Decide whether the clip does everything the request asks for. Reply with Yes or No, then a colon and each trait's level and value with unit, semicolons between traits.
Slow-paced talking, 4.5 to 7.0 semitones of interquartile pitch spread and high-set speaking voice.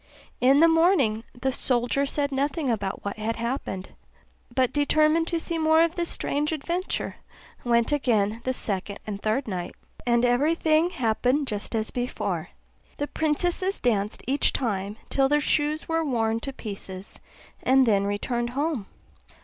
No: average, 155 wpm; wide, 5.5 semitones; very high, 260 Hz